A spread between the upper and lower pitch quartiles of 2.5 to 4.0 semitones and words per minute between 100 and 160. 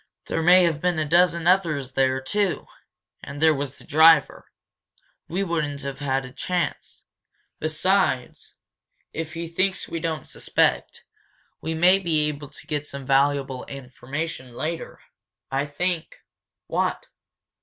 Yes: average, 3.5 semitones; average, 140 wpm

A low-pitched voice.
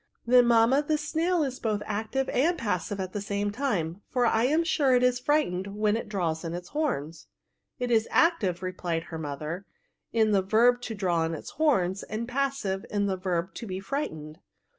No: high, 210 Hz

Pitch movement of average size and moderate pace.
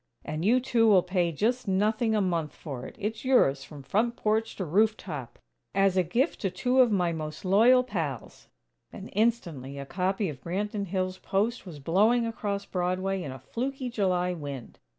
Yes: average, 4.9 semitones; average, 185 wpm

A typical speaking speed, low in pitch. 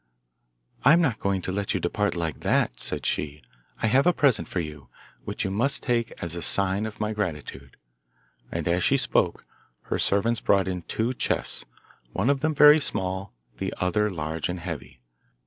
Yes: average, 185 wpm; low, 100 Hz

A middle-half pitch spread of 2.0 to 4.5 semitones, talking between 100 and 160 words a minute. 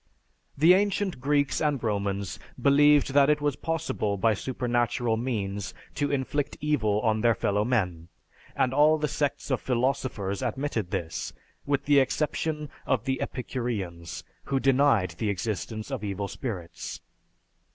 No: wide, 5.6 semitones; slow, 135 wpm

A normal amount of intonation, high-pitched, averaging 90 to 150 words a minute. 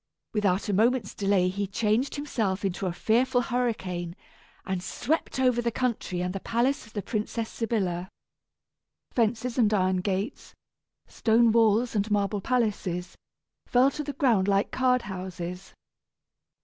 Yes: average, 4.2 semitones; high, 215 Hz; average, 140 wpm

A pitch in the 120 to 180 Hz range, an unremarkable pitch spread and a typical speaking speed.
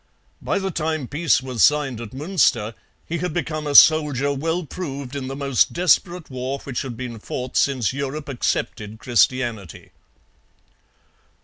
Yes: medium, 140 Hz; average, 3.8 semitones; average, 145 wpm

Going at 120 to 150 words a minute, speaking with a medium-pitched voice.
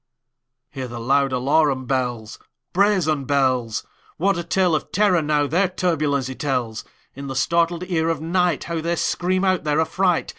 Yes: average, 140 wpm; medium, 155 Hz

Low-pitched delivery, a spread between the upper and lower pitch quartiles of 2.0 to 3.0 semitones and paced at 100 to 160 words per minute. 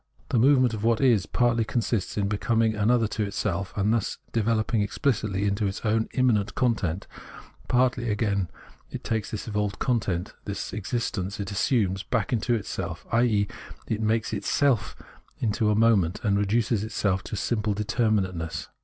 Yes: low, 110 Hz; narrow, 2.6 semitones; average, 155 wpm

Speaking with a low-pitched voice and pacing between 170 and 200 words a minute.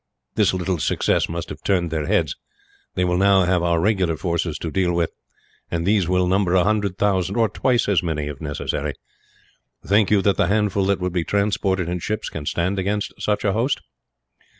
Yes: very low, 95 Hz; average, 195 wpm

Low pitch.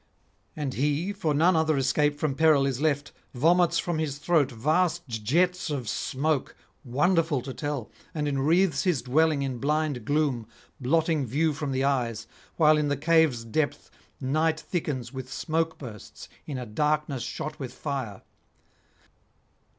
No: medium, 145 Hz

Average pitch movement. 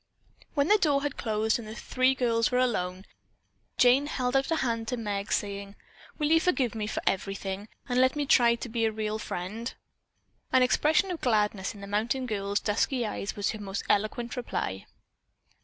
Yes: average, 3.9 semitones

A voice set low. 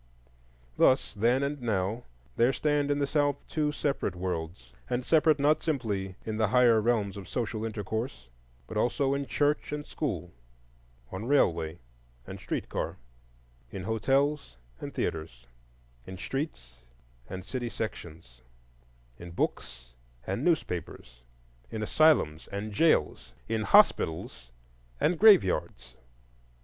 Yes: low, 110 Hz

